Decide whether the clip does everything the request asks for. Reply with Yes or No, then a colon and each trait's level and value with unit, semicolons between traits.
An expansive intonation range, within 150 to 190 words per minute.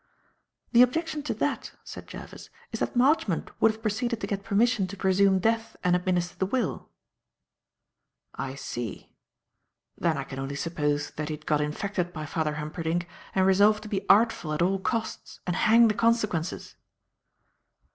Yes: wide, 5.7 semitones; average, 165 wpm